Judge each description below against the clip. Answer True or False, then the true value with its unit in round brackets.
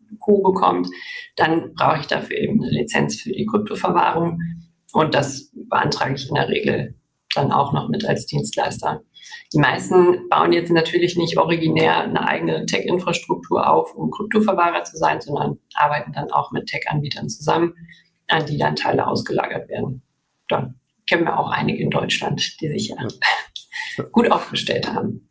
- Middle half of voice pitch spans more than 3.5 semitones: False (3.2 semitones)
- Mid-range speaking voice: True (170 Hz)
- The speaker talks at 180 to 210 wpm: False (155 wpm)